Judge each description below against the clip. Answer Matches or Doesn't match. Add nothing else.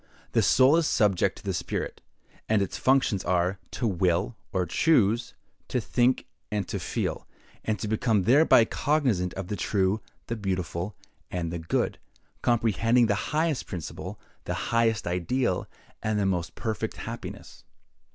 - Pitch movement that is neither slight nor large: Matches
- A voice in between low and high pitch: Doesn't match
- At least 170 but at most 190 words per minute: Doesn't match